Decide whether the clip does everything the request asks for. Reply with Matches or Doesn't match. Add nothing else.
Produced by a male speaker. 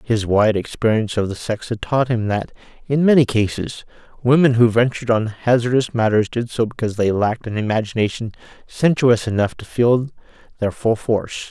Matches